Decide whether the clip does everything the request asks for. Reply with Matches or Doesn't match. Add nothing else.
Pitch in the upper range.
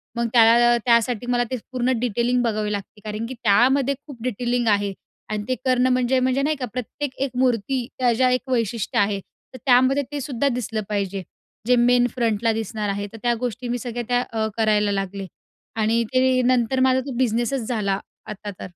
Matches